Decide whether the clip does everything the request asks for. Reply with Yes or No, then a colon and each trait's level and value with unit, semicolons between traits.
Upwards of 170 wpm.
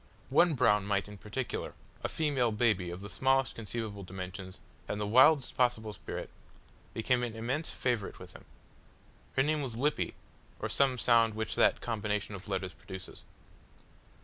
No: average, 155 wpm